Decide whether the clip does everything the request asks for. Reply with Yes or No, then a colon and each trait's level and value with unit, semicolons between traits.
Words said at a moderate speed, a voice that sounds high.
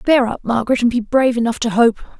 No: fast, 245 wpm; high, 240 Hz